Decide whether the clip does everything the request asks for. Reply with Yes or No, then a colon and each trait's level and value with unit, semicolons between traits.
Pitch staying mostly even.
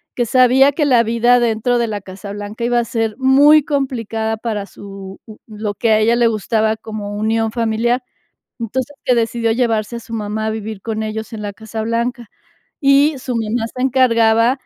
Yes: narrow, 2.2 semitones